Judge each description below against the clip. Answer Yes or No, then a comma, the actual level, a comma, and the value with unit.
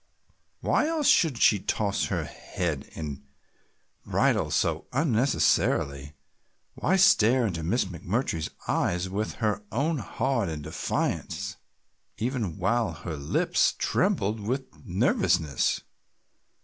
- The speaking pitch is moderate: No, low, 105 Hz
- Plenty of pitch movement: Yes, wide, 7.1 semitones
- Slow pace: Yes, slow, 110 wpm